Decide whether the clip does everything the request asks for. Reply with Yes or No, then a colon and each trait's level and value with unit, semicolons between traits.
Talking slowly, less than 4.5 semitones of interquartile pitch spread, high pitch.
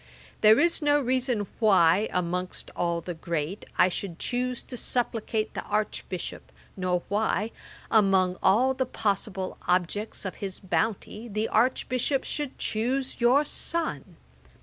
No: slow, 130 wpm; average, 5.3 semitones; high, 215 Hz